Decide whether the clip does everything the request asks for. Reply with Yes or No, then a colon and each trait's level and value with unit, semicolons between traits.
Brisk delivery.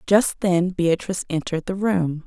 No: average, 160 wpm